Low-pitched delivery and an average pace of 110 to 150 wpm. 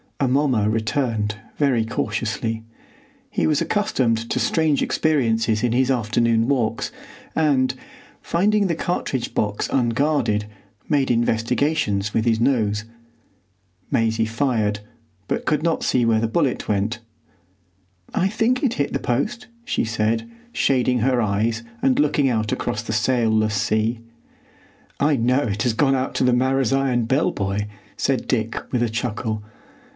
Yes: low, 120 Hz; average, 140 wpm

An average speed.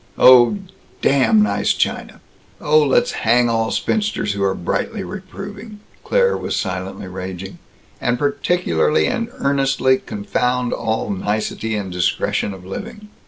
No: slow, 130 wpm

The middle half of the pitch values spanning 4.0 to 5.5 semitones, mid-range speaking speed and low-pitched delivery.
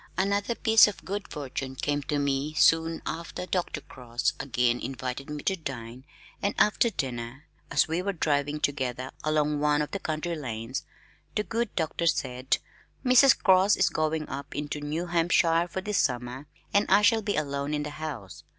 No: average, 5.0 semitones; average, 175 wpm; medium, 150 Hz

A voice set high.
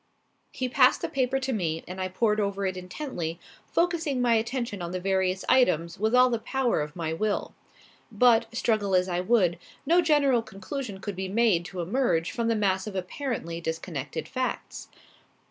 Yes: high, 210 Hz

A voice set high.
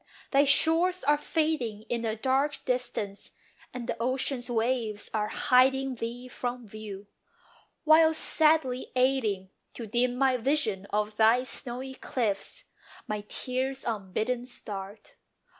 Yes: very high, 250 Hz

